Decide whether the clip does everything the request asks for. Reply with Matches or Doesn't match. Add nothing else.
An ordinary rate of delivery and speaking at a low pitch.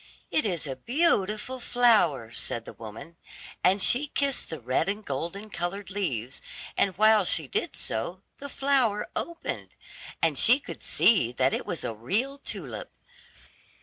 Doesn't match